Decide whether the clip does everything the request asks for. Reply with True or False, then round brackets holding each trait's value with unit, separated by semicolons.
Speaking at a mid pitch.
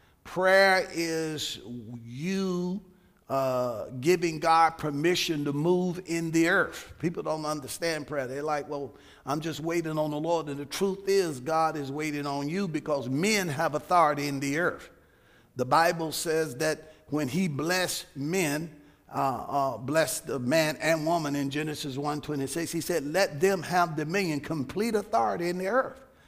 True (160 Hz)